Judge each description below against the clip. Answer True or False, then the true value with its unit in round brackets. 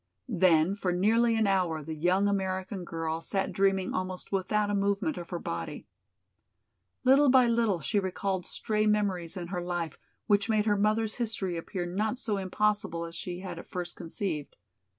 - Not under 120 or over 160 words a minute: False (170 wpm)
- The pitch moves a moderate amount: True (3.2 semitones)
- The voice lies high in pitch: True (195 Hz)